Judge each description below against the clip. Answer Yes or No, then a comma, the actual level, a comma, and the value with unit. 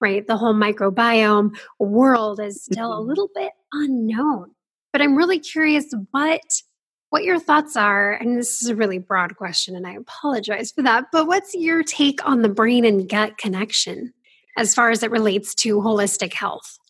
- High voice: Yes, high, 230 Hz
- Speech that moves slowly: No, average, 180 wpm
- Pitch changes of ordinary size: No, wide, 5.9 semitones